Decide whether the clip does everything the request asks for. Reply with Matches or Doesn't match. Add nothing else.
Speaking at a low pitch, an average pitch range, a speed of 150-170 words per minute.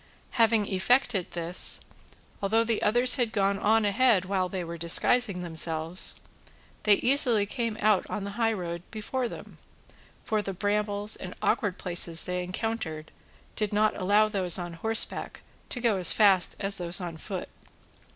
Doesn't match